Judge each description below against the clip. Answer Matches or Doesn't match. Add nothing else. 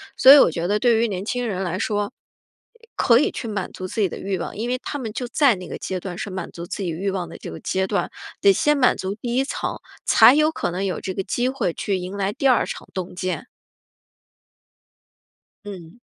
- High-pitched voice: Matches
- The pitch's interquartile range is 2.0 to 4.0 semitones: Doesn't match